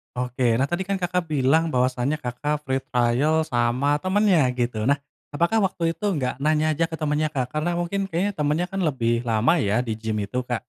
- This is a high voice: No, medium, 145 Hz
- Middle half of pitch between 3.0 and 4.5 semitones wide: No, average, 5.2 semitones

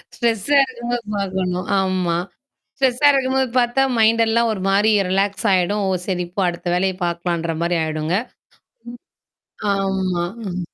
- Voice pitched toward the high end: Yes, high, 195 Hz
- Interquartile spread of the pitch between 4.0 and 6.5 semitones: Yes, average, 4.6 semitones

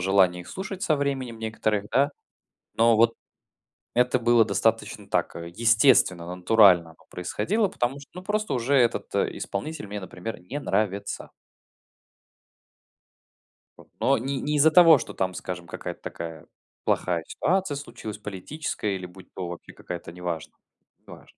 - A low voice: Yes, low, 110 Hz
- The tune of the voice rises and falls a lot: Yes, wide, 7.4 semitones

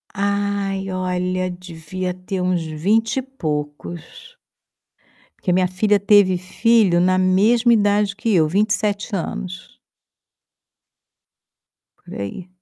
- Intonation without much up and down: Yes, narrow, 2.3 semitones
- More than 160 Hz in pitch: Yes, medium, 185 Hz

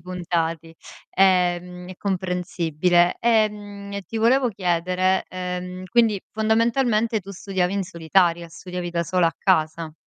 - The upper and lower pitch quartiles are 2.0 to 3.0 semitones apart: Yes, narrow, 2.6 semitones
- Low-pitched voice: No, medium, 185 Hz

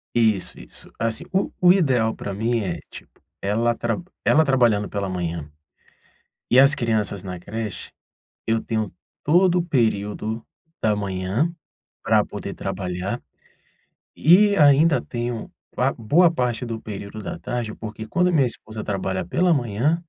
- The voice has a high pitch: No, low, 115 Hz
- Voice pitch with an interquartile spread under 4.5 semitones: No, wide, 5.4 semitones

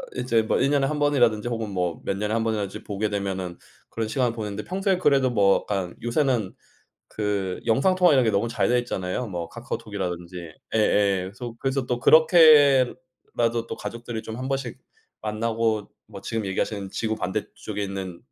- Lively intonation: No, average, 4.2 semitones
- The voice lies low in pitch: Yes, low, 115 Hz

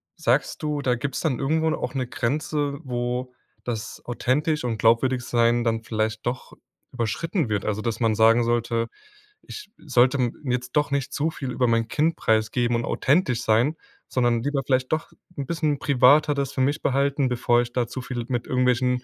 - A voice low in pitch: Yes, low, 125 Hz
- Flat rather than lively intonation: No, average, 3.1 semitones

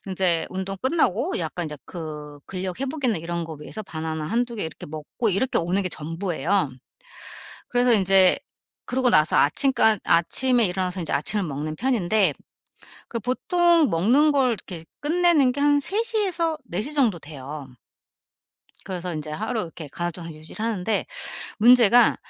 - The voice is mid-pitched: No, high, 195 Hz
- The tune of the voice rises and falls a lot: Yes, wide, 7.3 semitones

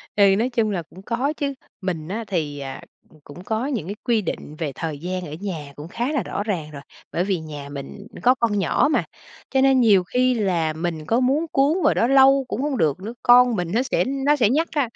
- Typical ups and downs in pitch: No, wide, 7.6 semitones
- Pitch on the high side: Yes, high, 205 Hz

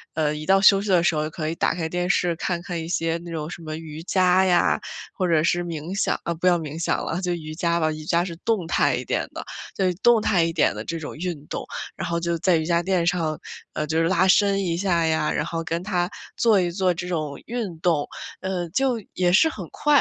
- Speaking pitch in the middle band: Yes, medium, 170 Hz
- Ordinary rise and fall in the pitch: No, narrow, 2.3 semitones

